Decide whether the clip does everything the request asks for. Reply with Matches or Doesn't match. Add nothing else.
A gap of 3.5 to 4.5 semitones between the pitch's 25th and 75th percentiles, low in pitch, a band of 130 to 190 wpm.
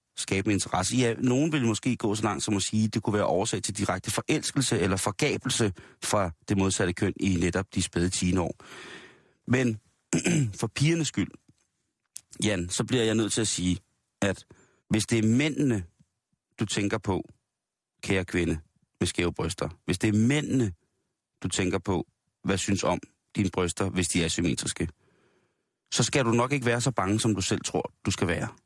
Matches